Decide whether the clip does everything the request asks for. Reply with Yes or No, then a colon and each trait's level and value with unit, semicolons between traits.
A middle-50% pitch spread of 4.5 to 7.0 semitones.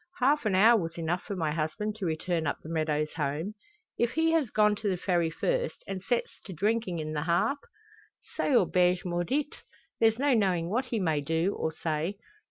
Yes: wide, 5.5 semitones